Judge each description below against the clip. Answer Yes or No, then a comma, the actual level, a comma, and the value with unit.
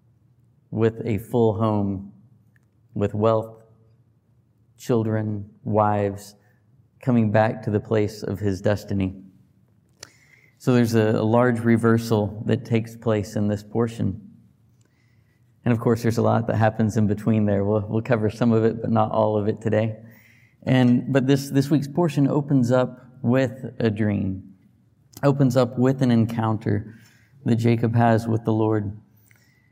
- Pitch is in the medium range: No, low, 115 Hz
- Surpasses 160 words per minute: No, average, 145 wpm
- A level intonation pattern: Yes, narrow, 2.0 semitones